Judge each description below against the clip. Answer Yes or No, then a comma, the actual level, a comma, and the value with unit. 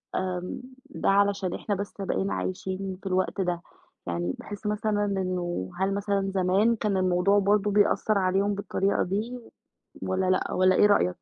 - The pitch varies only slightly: Yes, narrow, 1.8 semitones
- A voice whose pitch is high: Yes, high, 195 Hz